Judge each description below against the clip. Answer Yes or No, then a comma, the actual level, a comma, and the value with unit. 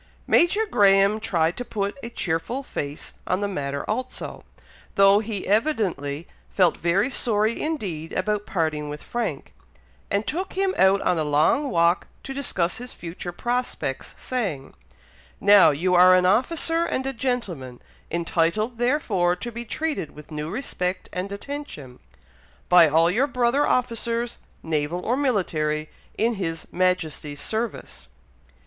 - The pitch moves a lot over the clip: Yes, wide, 6.5 semitones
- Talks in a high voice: Yes, high, 195 Hz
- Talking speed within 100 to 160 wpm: Yes, average, 140 wpm